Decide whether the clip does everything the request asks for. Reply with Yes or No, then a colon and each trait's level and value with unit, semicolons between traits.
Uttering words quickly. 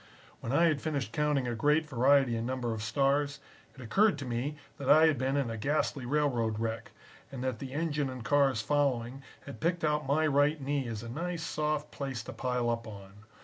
Yes: fast, 210 wpm